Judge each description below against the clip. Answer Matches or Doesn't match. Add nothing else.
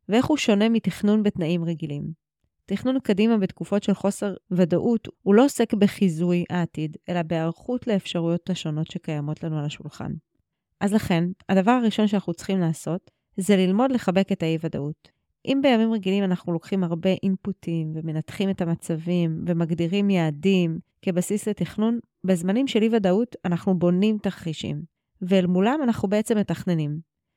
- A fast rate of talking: Doesn't match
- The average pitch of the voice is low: Doesn't match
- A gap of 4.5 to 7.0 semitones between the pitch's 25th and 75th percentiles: Doesn't match